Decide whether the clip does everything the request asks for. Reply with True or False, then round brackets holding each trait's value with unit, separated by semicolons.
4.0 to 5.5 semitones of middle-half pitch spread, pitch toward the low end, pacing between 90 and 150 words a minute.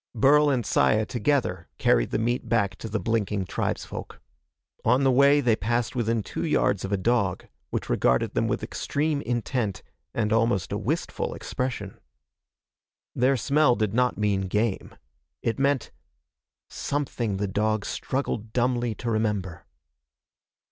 False (3.5 semitones; 115 Hz; 140 wpm)